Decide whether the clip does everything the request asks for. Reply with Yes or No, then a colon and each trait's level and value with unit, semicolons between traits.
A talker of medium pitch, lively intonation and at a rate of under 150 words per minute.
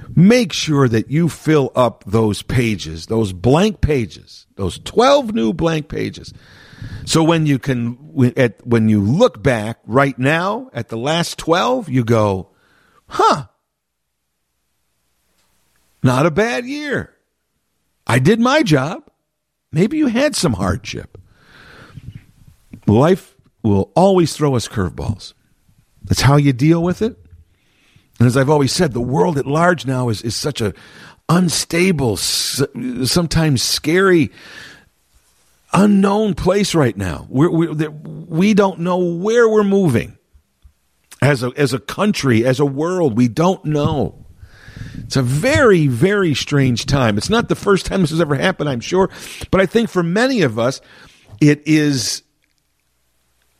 Yes: medium, 145 Hz; wide, 7.4 semitones; average, 140 wpm